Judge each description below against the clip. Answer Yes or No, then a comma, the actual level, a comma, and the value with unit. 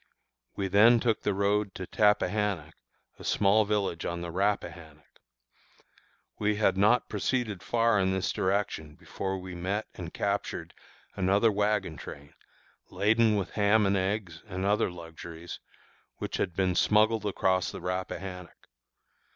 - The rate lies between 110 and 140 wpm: Yes, slow, 135 wpm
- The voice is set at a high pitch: No, low, 100 Hz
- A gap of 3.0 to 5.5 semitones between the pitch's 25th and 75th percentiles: No, narrow, 2.5 semitones